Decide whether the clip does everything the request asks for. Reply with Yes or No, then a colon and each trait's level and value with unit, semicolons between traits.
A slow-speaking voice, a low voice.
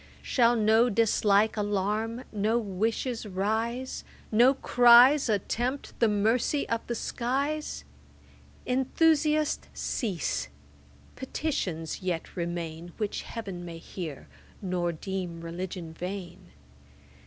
No: slow, 95 wpm; high, 215 Hz